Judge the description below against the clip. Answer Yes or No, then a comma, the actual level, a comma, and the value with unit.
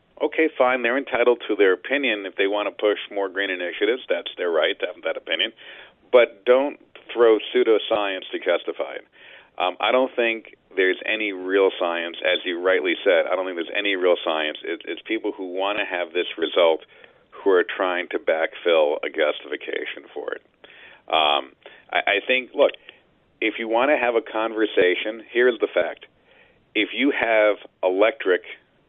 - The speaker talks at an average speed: Yes, average, 175 wpm